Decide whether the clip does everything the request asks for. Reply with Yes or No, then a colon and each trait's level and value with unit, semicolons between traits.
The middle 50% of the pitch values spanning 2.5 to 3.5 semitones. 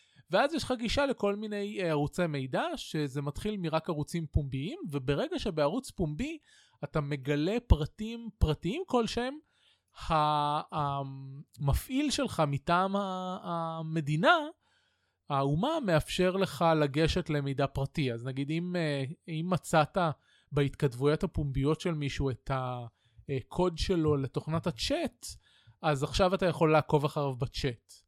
No: average, 4.4 semitones